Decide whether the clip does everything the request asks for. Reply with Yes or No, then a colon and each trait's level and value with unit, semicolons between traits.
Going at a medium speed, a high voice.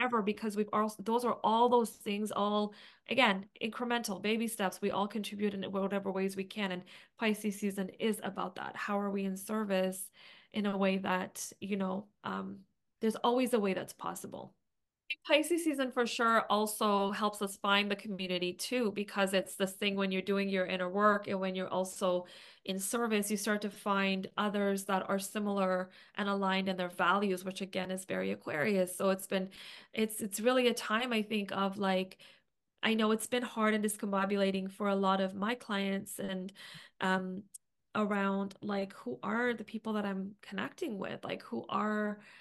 Yes: average, 185 wpm; high, 200 Hz